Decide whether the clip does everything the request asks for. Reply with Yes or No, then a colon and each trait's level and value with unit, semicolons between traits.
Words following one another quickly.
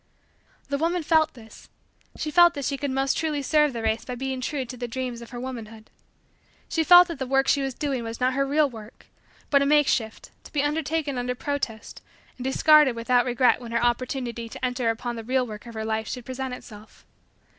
Yes: fast, 215 wpm